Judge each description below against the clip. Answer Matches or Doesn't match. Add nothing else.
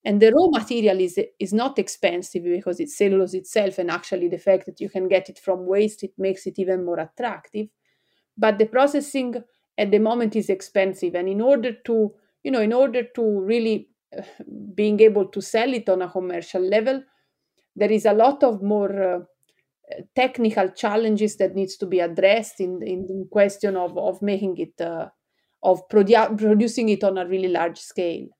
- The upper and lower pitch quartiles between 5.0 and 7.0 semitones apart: Doesn't match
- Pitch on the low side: Doesn't match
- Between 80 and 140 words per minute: Doesn't match